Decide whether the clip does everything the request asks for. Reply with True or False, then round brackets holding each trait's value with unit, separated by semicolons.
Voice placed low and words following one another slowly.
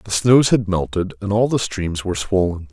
False (100 Hz; 220 wpm)